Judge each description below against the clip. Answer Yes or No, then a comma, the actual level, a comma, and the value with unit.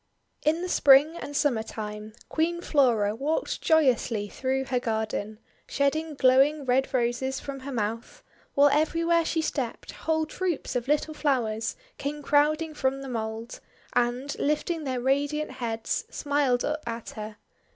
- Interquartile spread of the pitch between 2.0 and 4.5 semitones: Yes, average, 4.2 semitones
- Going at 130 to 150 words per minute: Yes, average, 145 wpm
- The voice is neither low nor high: No, very high, 270 Hz